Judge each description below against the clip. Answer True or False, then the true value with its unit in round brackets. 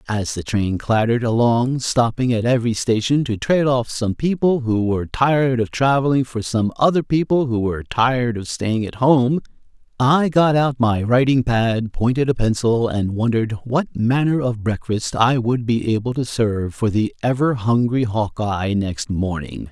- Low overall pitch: True (120 Hz)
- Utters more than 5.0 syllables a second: False (4.7 syllables/s)